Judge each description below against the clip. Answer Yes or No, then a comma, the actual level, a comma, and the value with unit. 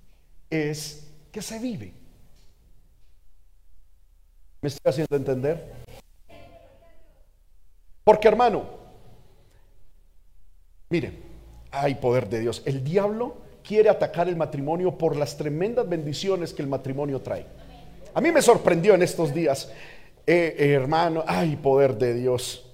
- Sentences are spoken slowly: Yes, slow, 115 wpm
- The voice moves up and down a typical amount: No, wide, 6.6 semitones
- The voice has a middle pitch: Yes, medium, 145 Hz